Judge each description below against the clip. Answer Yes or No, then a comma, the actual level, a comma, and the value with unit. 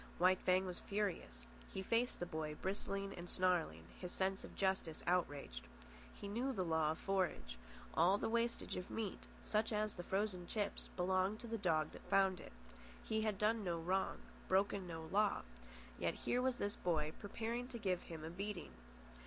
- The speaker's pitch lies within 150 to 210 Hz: Yes, high, 190 Hz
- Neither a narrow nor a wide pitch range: Yes, average, 3.3 semitones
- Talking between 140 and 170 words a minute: No, average, 180 wpm